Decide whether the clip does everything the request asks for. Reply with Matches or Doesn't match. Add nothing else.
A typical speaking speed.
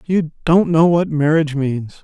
Matches